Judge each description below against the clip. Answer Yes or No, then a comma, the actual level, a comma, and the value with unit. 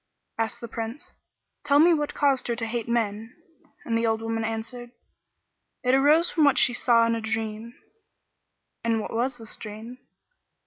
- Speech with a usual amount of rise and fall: No, narrow, 2.2 semitones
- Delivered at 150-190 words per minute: Yes, average, 170 wpm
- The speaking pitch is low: No, high, 230 Hz